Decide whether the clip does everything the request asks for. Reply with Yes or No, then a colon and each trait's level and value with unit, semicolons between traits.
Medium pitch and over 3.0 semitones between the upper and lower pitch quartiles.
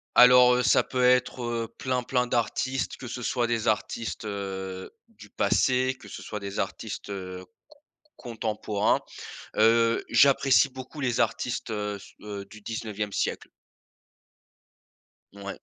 No: low, 115 Hz; average, 3.4 semitones